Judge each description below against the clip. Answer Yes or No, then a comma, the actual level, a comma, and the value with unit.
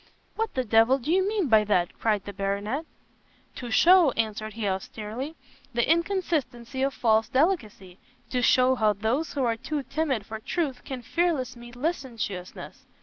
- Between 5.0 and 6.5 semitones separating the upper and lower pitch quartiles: Yes, wide, 5.6 semitones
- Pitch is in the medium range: No, high, 245 Hz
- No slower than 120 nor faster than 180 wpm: Yes, average, 165 wpm